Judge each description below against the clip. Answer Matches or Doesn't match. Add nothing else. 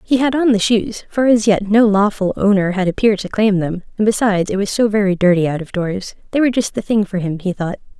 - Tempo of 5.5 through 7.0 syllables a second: Matches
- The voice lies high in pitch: Matches